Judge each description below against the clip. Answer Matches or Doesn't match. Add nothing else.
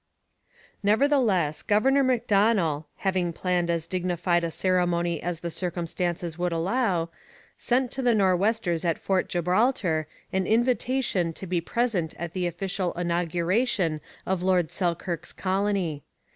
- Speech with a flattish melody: Doesn't match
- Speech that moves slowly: Matches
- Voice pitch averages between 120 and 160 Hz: Doesn't match